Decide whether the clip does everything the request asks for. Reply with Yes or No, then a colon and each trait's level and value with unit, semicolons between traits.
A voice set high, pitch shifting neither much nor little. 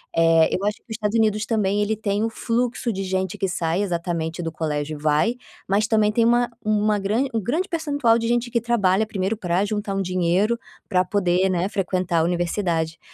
Yes: high, 200 Hz; average, 4.1 semitones